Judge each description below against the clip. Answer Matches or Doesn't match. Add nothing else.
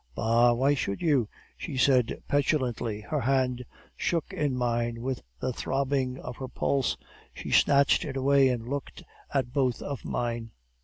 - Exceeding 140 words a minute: Matches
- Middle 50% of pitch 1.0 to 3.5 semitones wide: Matches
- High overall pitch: Doesn't match